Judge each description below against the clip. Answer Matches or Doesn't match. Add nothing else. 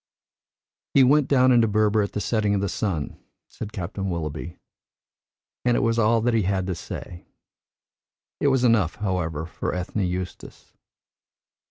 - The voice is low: Matches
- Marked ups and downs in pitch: Doesn't match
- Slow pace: Doesn't match